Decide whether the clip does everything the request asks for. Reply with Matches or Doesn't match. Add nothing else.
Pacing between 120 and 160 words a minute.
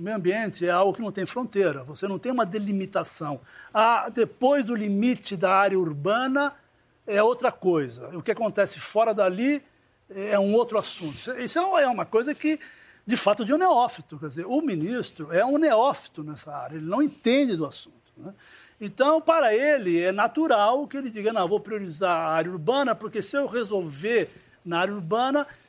Doesn't match